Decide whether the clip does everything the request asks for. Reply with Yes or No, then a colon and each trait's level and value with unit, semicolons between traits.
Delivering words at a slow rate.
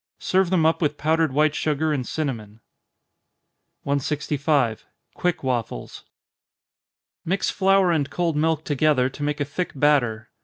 Yes: slow, 130 wpm